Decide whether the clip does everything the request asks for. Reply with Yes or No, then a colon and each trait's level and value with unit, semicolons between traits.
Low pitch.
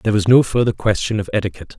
Yes: low, 105 Hz